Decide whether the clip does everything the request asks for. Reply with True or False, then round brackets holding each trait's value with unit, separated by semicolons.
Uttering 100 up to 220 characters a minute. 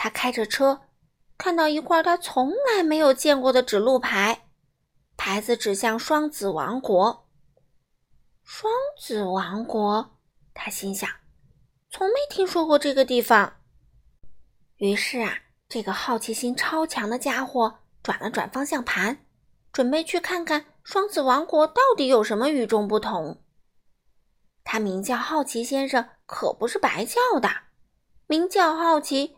True (200 characters per minute)